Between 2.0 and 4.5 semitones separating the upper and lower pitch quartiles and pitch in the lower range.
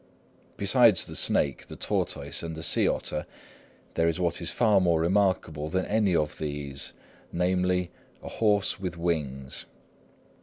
Yes: average, 3.6 semitones; very low, 85 Hz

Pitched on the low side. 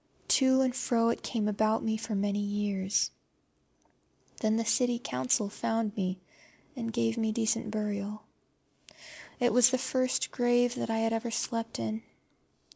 No: high, 225 Hz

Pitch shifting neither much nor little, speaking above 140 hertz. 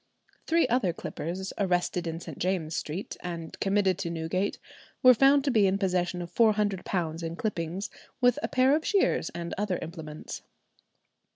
Yes: average, 4.2 semitones; medium, 185 Hz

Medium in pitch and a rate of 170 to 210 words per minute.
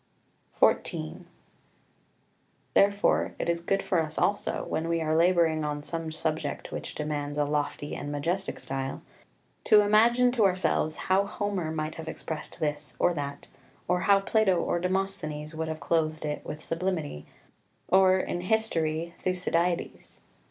No: medium, 165 Hz; average, 155 wpm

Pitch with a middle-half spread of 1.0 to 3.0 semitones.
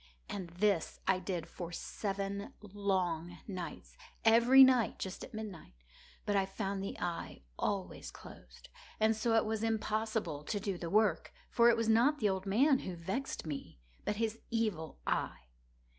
No: average, 3.7 semitones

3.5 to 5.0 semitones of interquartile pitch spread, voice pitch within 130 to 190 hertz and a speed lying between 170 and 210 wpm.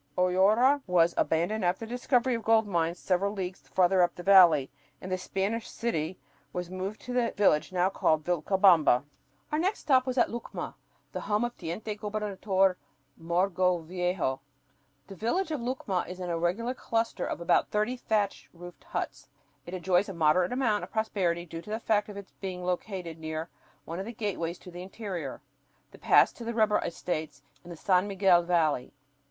Yes: average, 3.8 semitones; medium, 185 Hz; average, 180 wpm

